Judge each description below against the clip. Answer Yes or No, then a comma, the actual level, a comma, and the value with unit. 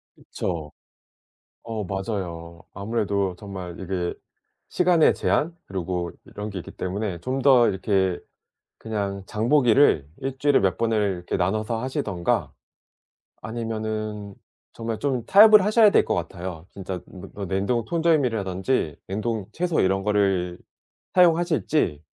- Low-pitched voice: Yes, low, 105 Hz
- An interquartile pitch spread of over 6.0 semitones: No, average, 5.2 semitones